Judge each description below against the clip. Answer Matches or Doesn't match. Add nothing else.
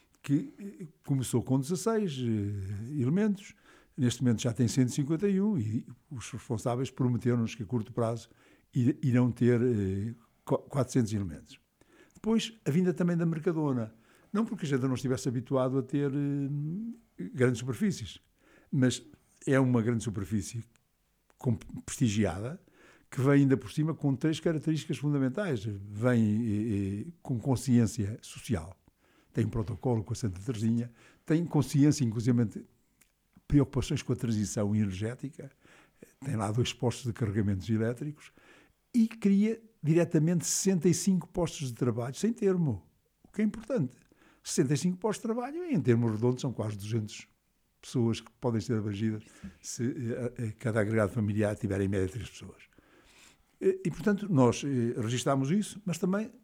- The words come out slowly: Doesn't match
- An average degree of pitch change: Doesn't match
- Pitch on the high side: Doesn't match